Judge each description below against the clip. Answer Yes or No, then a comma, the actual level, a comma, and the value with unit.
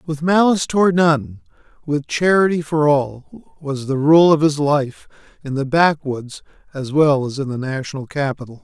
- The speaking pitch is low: No, medium, 150 Hz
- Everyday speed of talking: Yes, average, 165 wpm